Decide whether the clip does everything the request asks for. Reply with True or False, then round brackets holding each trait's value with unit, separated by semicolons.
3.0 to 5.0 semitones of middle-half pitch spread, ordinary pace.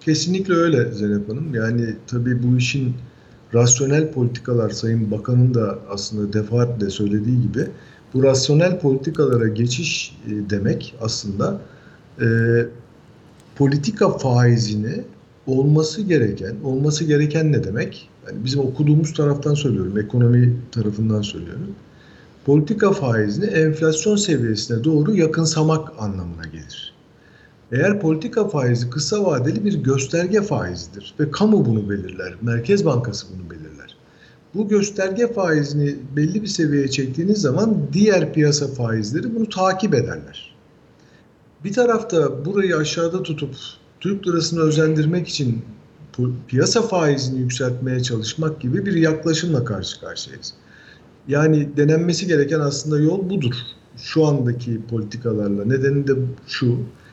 False (5.4 semitones; 115 wpm)